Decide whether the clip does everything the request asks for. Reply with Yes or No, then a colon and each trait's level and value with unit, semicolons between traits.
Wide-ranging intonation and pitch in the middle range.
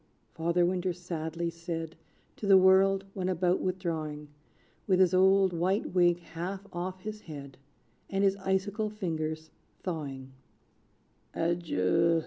No: narrow, 2.6 semitones; medium, 175 Hz